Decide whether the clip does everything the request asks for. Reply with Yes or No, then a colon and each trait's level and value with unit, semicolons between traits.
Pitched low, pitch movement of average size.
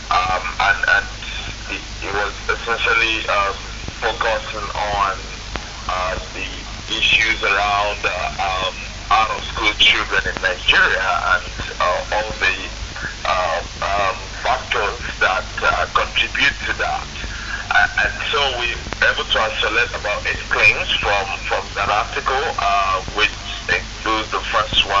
No: low, 105 Hz; narrow, 2.3 semitones